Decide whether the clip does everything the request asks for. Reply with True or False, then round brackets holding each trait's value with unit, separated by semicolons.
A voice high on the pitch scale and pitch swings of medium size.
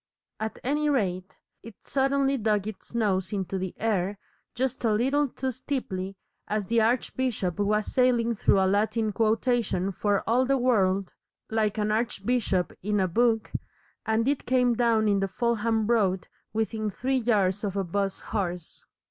True (220 Hz; 3.6 semitones)